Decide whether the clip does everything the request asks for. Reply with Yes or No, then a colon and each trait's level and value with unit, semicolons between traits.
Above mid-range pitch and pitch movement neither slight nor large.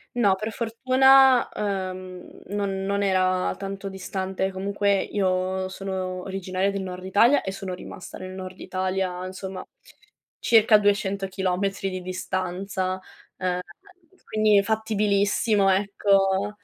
No: high, 195 Hz; narrow, 1.5 semitones